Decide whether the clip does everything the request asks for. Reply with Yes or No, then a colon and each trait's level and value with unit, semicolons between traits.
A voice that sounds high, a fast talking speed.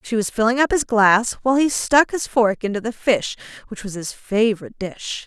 Yes: high, 225 Hz; fast, 215 wpm